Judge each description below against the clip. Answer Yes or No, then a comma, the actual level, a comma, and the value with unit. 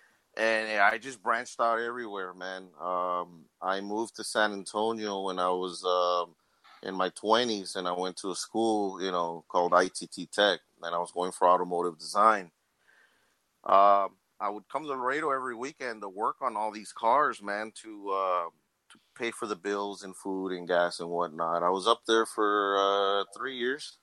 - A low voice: Yes, very low, 95 Hz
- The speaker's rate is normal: Yes, average, 185 wpm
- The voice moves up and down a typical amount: Yes, average, 3.0 semitones